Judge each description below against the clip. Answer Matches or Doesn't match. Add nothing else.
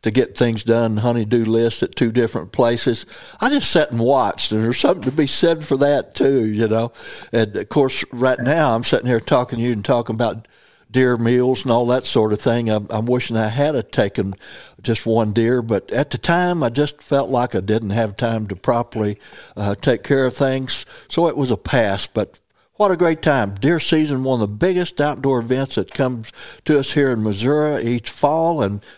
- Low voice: Matches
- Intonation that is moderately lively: Matches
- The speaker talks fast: Matches